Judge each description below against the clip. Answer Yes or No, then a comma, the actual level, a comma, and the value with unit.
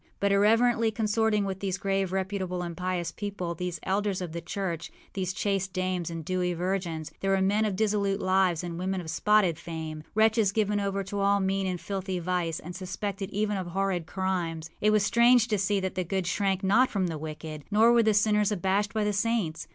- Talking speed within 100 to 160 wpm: No, fast, 205 wpm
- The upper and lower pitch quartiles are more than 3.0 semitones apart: No, narrow, 2.6 semitones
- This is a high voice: Yes, high, 195 Hz